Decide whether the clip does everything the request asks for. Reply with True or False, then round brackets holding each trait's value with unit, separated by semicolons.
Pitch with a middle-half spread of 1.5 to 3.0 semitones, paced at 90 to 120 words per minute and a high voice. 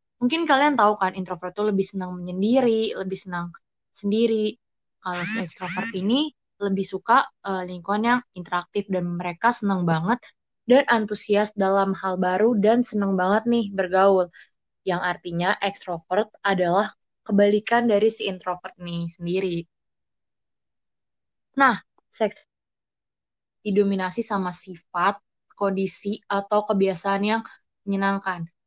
True (2.7 semitones; 115 wpm; 195 Hz)